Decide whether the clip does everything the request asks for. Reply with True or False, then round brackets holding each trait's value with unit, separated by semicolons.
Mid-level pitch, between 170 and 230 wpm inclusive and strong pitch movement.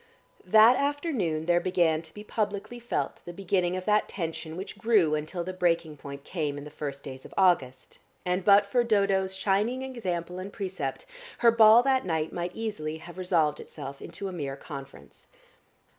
False (180 Hz; 175 wpm; 4.7 semitones)